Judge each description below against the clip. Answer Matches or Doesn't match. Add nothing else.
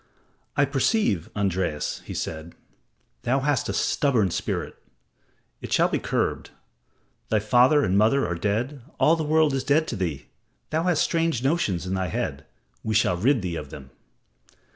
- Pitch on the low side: Matches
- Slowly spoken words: Doesn't match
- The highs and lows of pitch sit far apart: Matches